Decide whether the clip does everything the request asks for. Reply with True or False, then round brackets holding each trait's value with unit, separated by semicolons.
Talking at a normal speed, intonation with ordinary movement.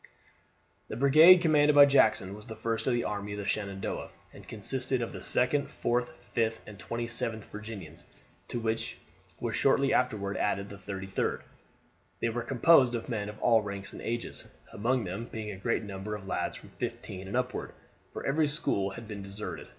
True (180 wpm; 3.6 semitones)